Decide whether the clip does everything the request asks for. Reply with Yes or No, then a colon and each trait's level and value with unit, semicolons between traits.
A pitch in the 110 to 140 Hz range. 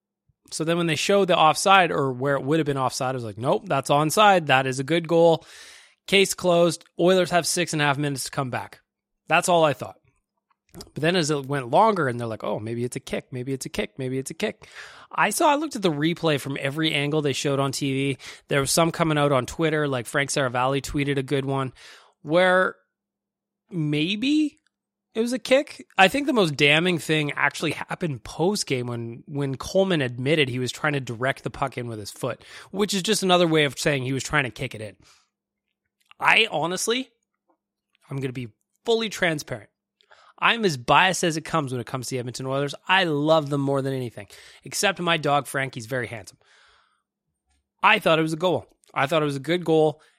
No: medium, 150 Hz